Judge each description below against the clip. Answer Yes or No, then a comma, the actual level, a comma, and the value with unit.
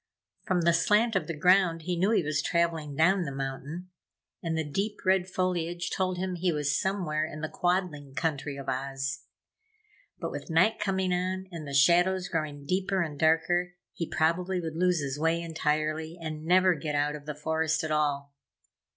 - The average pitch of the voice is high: No, medium, 165 Hz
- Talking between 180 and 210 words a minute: Yes, average, 185 wpm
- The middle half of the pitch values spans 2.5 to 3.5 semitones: Yes, average, 3.2 semitones